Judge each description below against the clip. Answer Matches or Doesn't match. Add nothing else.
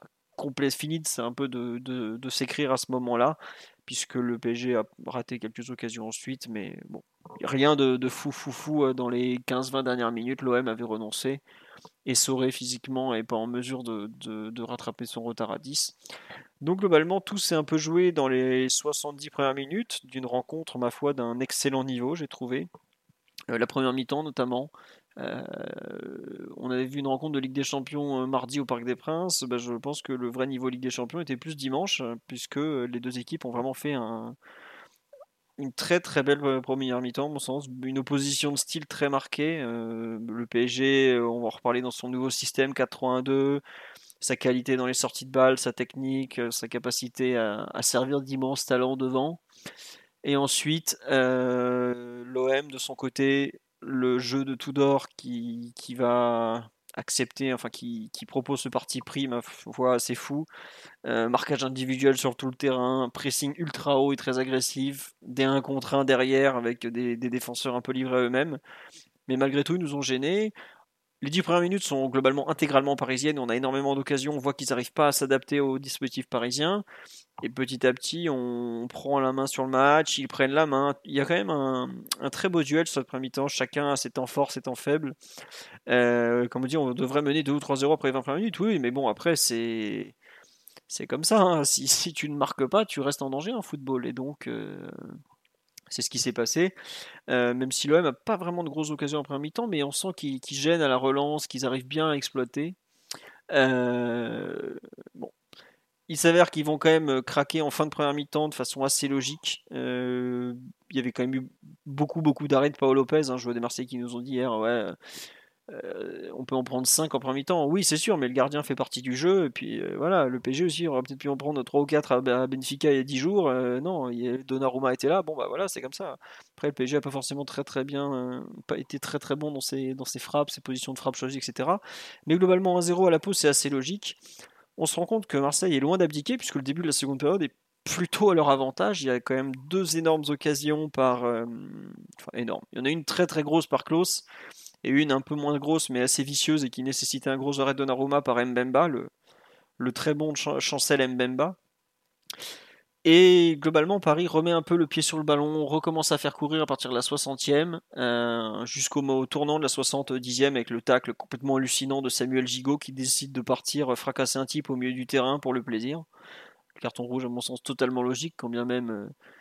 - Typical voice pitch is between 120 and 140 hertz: Matches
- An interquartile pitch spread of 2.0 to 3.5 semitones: Matches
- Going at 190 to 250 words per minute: Matches